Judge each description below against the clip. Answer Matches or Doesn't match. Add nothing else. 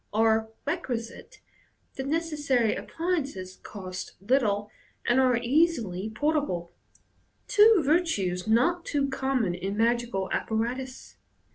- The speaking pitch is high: Matches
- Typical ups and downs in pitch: Doesn't match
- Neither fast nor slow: Doesn't match